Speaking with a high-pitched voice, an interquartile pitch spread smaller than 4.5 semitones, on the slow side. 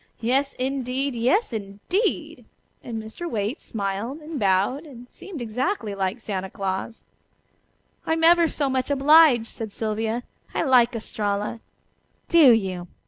No: high, 240 Hz; average, 5.2 semitones; slow, 130 wpm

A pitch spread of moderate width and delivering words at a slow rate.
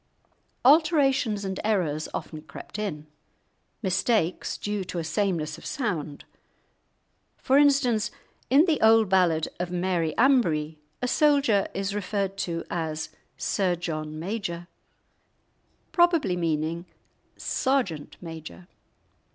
No: wide, 5.9 semitones; slow, 110 wpm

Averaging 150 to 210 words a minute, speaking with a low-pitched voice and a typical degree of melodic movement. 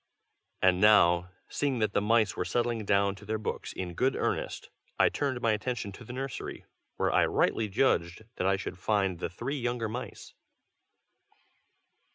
Yes: average, 170 wpm; low, 105 Hz; average, 4.0 semitones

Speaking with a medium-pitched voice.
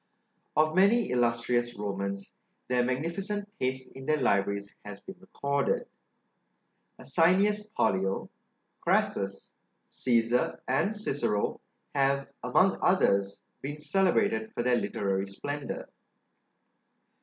No: low, 125 Hz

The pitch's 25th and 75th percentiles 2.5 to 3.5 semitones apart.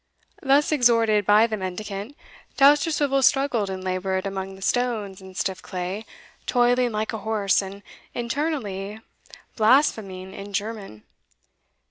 No: average, 4.2 semitones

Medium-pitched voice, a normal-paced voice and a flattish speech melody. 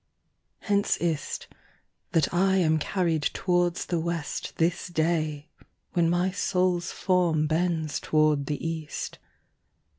No: medium, 170 Hz; slow, 110 wpm; narrow, 2.3 semitones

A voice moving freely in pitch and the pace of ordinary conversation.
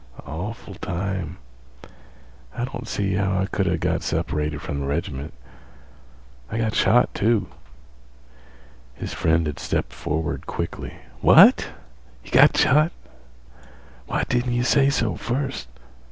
No: wide, 6.5 semitones; slow, 125 wpm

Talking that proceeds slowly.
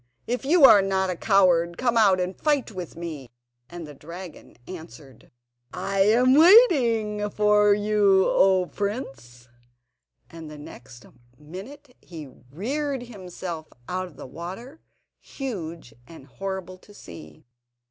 Yes: slow, 130 wpm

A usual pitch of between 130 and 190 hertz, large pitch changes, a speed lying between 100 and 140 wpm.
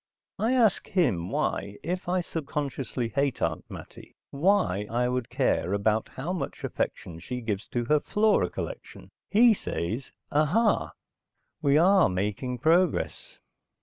Yes: medium, 140 Hz; wide, 8.5 semitones; slow, 135 wpm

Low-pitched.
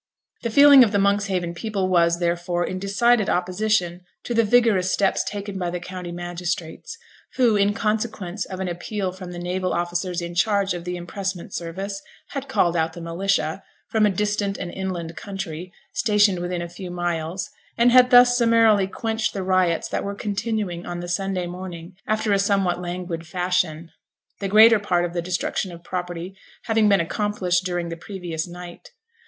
No: medium, 185 Hz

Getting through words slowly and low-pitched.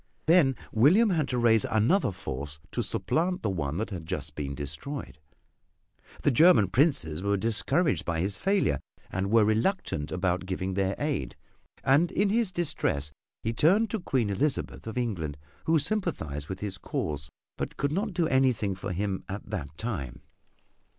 No: average, 165 wpm; low, 110 Hz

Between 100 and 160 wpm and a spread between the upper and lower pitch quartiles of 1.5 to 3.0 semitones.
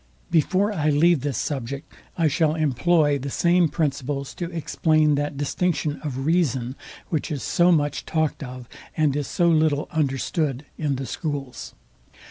Yes: average, 150 wpm; average, 2.7 semitones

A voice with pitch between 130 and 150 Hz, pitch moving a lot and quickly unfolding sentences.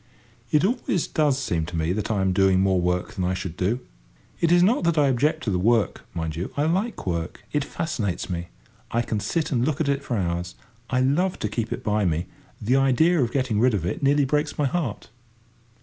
No: low, 120 Hz; wide, 8.1 semitones; fast, 225 wpm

